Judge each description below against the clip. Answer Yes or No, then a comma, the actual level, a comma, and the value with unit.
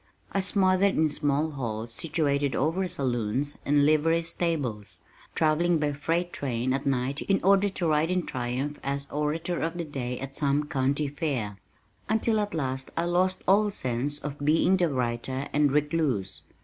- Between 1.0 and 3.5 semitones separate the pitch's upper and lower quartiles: No, average, 4.1 semitones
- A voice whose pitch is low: No, medium, 145 Hz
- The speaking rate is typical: Yes, average, 160 wpm